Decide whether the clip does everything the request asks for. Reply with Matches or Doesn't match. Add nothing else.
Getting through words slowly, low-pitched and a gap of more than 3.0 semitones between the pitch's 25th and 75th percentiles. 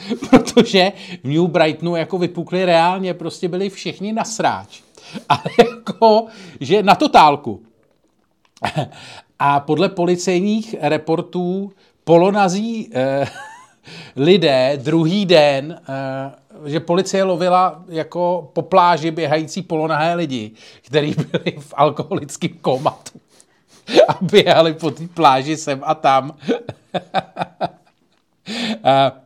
Doesn't match